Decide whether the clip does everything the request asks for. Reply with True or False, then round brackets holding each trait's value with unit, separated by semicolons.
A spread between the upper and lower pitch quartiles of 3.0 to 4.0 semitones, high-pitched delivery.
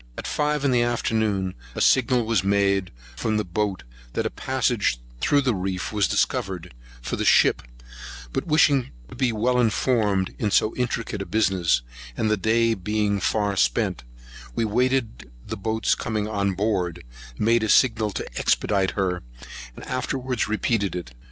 False (3.6 semitones; 110 Hz)